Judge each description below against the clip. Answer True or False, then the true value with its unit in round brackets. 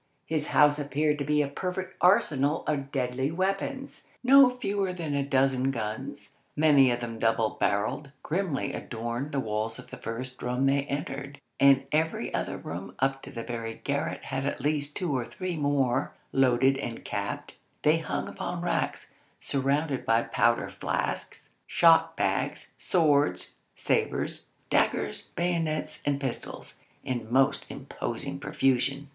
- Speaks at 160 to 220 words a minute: False (145 wpm)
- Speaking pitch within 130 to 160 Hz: True (140 Hz)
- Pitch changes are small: False (3.5 semitones)